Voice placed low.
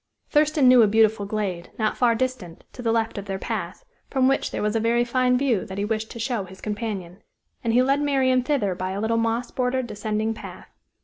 No: high, 225 Hz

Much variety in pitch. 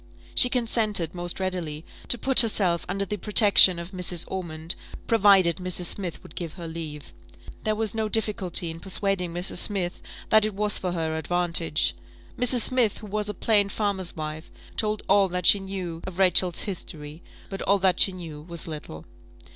No: average, 3.5 semitones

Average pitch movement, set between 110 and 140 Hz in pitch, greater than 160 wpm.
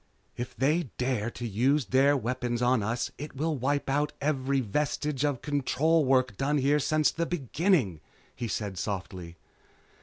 No: average, 3.7 semitones; low, 135 Hz; average, 155 wpm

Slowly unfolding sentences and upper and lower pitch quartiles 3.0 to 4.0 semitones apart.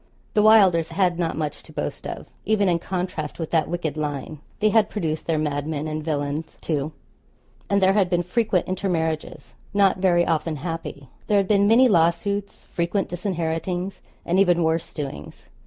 No: average, 170 wpm; average, 3.6 semitones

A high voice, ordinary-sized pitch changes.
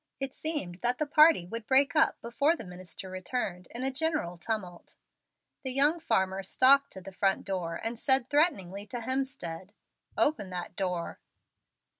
No: high, 225 Hz; wide, 6.7 semitones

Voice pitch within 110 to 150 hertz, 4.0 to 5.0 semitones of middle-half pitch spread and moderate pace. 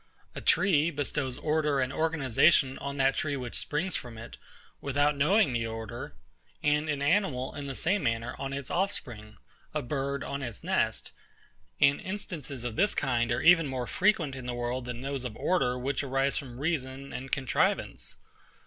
No: low, 135 Hz; average, 3.3 semitones; average, 170 wpm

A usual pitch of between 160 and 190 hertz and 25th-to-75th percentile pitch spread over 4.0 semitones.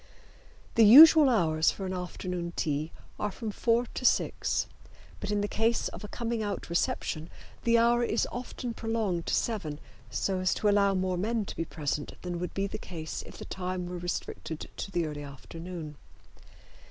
Yes: medium, 185 Hz; average, 4.8 semitones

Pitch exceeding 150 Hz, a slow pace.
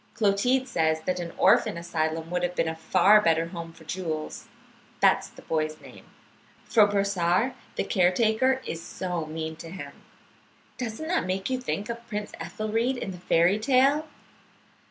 No: medium, 185 Hz; average, 165 wpm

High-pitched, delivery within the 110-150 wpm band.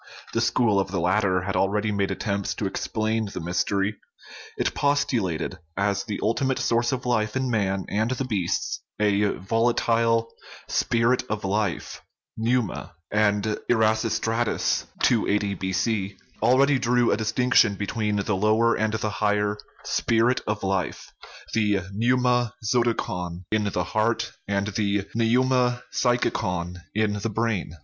No: low, 110 Hz; average, 140 wpm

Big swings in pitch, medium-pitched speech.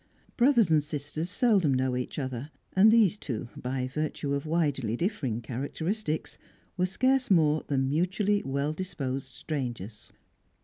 Yes: wide, 6.1 semitones; medium, 150 Hz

